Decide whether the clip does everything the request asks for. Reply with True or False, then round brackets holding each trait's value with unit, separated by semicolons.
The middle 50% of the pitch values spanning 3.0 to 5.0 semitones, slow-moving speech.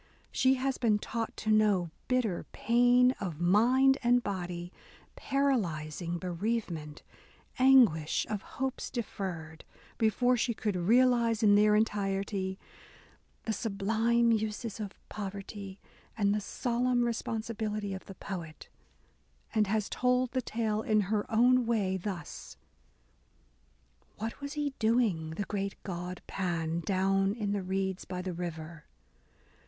True (3.9 semitones; 125 wpm)